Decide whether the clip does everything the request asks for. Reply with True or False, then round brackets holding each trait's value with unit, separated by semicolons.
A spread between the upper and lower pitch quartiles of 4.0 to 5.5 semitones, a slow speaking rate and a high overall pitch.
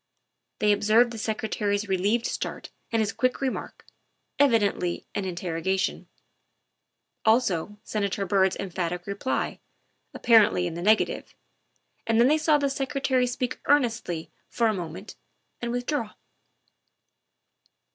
True (4.4 semitones; 125 wpm; 215 Hz)